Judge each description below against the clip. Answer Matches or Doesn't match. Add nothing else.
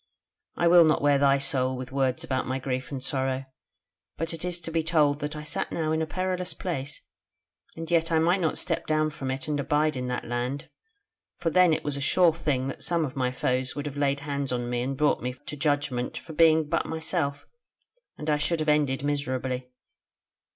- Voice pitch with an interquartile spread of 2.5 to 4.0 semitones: Matches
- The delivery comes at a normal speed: Doesn't match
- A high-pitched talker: Doesn't match